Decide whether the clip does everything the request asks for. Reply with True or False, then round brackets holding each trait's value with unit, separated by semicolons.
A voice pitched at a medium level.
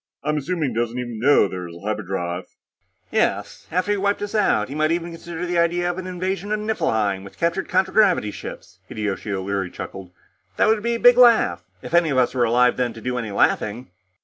True (145 Hz)